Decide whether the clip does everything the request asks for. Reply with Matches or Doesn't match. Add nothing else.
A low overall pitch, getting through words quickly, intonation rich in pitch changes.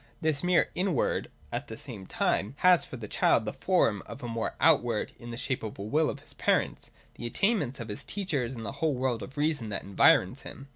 Matches